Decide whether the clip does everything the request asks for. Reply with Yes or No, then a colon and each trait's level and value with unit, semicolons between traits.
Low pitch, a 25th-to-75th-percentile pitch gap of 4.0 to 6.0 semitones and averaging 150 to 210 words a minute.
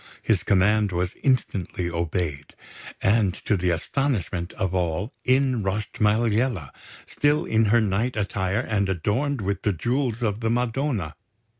No: low, 105 Hz; average, 4.5 semitones; average, 140 wpm